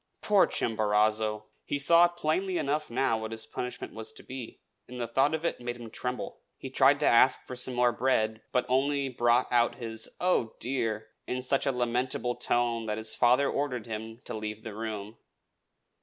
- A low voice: Yes, low, 120 Hz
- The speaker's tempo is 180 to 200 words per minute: Yes, average, 185 wpm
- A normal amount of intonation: Yes, average, 3.2 semitones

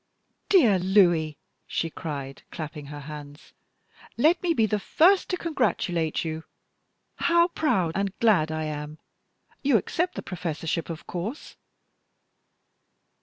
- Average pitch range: No, wide, 8.5 semitones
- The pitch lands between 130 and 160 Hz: No, medium, 175 Hz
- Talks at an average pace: No, slow, 120 wpm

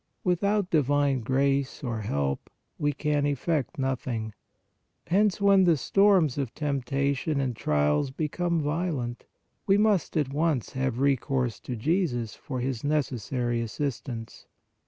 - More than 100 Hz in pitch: Yes, medium, 140 Hz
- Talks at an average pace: No, slow, 130 wpm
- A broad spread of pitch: No, average, 4.5 semitones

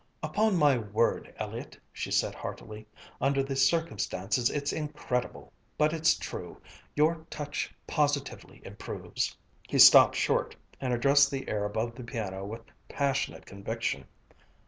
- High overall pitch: No, low, 130 Hz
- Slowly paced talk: Yes, slow, 130 wpm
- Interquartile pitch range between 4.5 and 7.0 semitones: Yes, average, 4.9 semitones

